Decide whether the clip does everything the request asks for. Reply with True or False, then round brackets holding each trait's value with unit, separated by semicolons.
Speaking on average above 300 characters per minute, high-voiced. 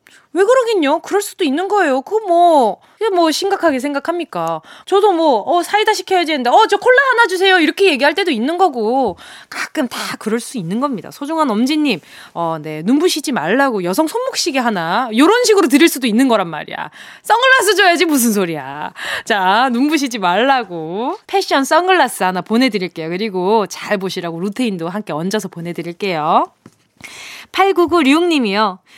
True (360 characters per minute; 280 Hz)